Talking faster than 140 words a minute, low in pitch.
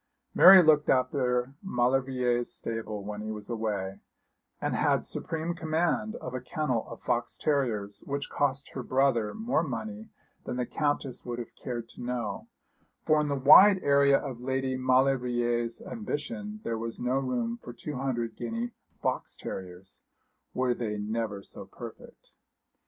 Yes: average, 150 wpm; low, 125 Hz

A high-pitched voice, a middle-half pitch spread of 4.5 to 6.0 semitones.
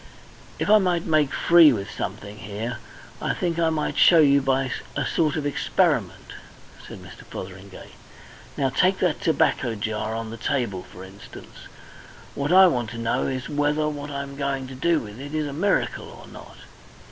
No: medium, 140 Hz; wide, 5.6 semitones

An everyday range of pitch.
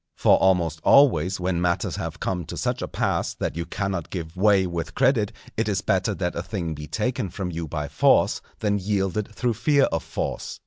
Yes: average, 3.8 semitones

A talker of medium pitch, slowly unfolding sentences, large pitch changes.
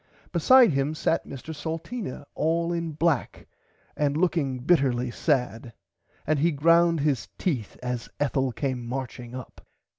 No: medium, 145 Hz; slow, 130 wpm; average, 4.7 semitones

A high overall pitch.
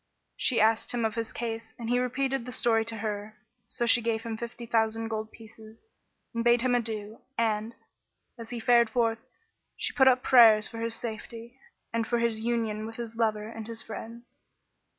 Yes: high, 230 Hz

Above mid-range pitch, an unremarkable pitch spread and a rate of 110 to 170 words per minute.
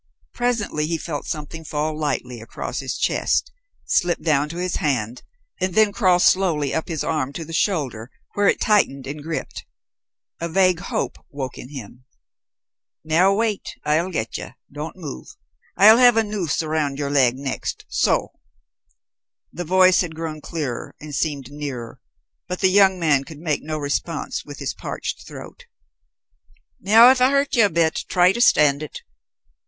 No: medium, 160 Hz; average, 4.5 semitones; average, 165 wpm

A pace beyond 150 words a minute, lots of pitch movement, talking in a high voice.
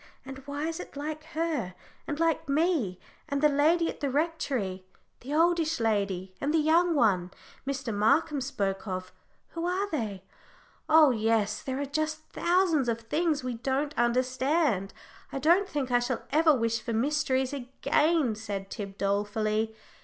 Yes: average, 160 wpm; wide, 5.9 semitones; very high, 275 Hz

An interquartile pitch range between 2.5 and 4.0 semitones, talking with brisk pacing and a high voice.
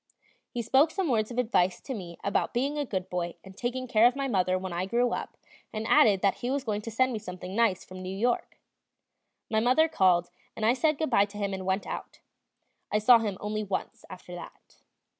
No: average, 4.6 semitones; fast, 225 wpm; high, 215 Hz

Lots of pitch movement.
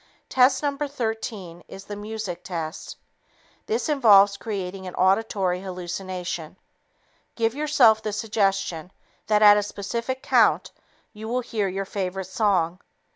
No: average, 3.3 semitones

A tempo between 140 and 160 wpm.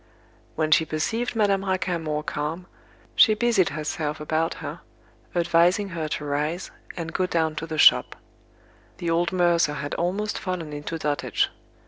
Yes: average, 150 wpm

